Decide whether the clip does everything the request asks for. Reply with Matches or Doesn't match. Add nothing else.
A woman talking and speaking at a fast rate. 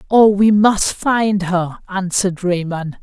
Doesn't match